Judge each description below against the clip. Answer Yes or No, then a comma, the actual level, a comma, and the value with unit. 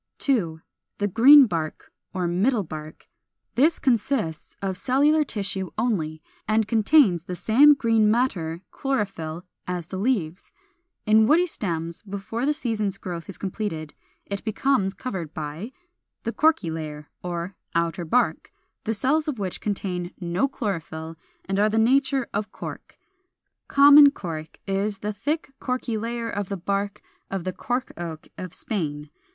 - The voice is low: No, high, 200 Hz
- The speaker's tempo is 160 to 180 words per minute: No, average, 150 wpm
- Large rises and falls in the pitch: Yes, wide, 6.0 semitones